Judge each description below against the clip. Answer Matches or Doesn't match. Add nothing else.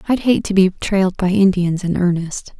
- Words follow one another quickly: Matches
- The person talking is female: Matches